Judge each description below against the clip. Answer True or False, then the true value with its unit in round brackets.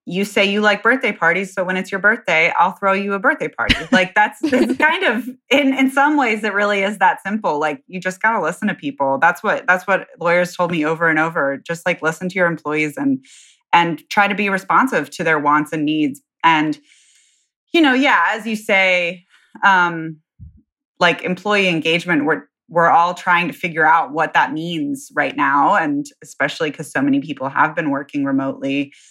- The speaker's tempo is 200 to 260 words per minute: True (205 wpm)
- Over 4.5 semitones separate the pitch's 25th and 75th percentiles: True (4.9 semitones)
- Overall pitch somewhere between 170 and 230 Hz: True (185 Hz)